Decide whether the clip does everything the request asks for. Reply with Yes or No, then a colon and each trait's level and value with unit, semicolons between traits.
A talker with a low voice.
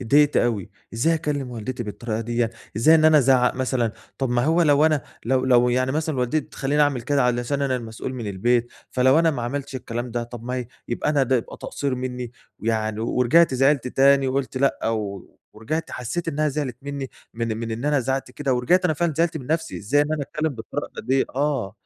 Yes: low, 130 Hz